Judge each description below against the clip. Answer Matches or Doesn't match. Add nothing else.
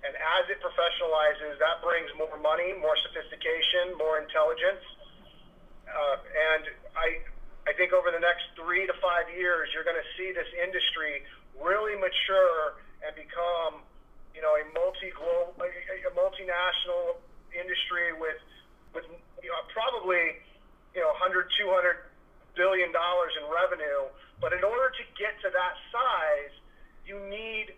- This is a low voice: Doesn't match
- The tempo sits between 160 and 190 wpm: Doesn't match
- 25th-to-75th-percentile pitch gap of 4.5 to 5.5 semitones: Doesn't match